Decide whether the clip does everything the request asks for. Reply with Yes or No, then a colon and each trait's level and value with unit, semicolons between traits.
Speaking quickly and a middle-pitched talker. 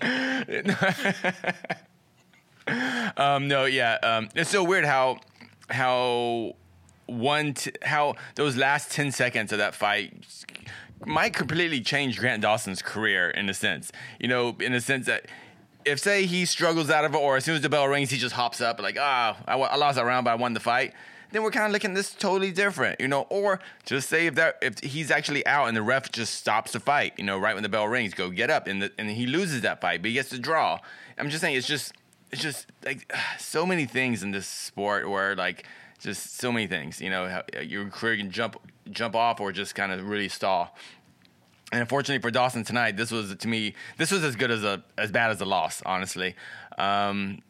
No: fast, 215 wpm; low, 125 Hz